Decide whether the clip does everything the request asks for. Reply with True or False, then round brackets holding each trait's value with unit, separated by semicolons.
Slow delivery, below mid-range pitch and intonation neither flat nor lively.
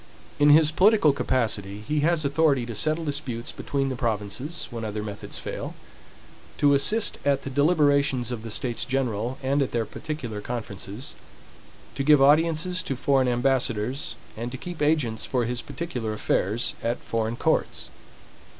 False (155 wpm; 130 Hz; 4.3 semitones)